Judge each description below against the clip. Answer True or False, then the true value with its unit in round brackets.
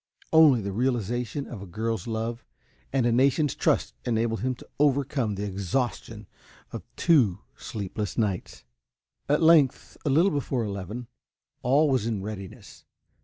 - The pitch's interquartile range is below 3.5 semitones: False (4.7 semitones)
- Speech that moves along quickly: False (140 wpm)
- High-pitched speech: False (120 Hz)